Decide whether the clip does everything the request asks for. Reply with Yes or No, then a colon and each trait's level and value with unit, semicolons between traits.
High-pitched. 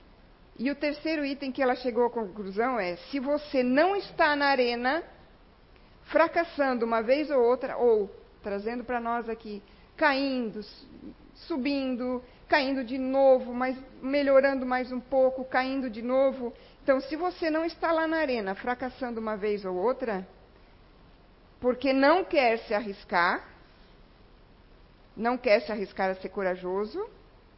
Yes: very high, 255 Hz